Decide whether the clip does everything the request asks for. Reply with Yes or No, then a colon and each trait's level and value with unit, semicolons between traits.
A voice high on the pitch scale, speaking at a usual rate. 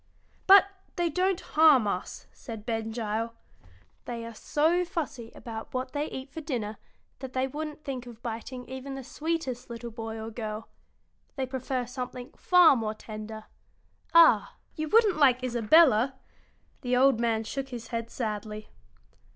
Yes: very high, 250 Hz; average, 150 wpm